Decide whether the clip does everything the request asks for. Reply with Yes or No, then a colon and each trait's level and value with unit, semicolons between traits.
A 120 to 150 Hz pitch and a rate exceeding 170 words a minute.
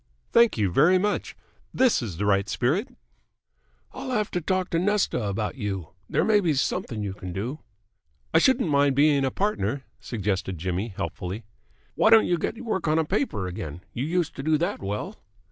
Yes: medium, 140 Hz; average, 185 wpm